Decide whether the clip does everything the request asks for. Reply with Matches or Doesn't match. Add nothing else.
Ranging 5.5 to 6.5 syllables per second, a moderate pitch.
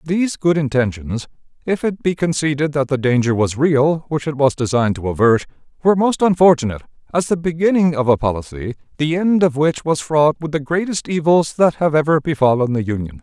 Matches